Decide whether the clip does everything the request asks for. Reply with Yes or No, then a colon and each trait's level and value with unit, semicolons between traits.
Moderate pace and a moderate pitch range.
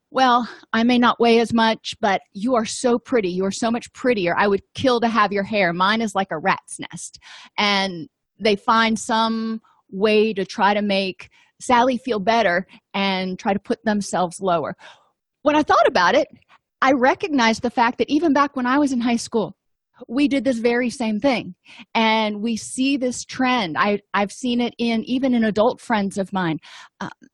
Yes: average, 195 wpm; average, 3.6 semitones